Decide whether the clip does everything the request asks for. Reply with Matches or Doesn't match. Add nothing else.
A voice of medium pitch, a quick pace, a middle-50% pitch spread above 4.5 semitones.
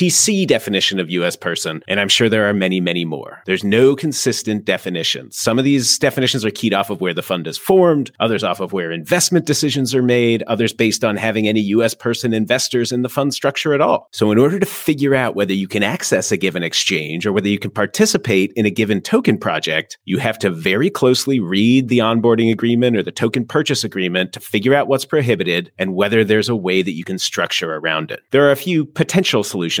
Doesn't match